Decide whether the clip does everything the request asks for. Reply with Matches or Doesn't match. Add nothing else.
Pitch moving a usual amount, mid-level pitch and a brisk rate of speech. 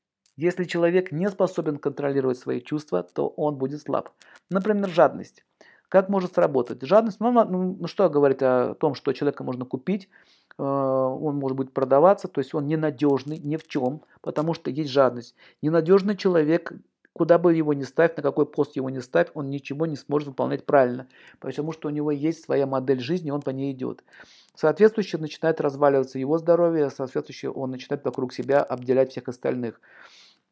Matches